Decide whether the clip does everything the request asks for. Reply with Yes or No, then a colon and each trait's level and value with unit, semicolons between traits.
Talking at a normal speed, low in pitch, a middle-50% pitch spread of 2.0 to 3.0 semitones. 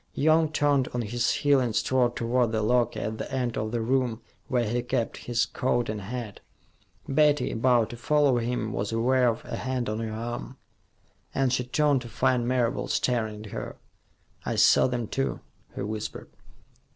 Yes: average, 180 wpm; low, 120 Hz; narrow, 2.4 semitones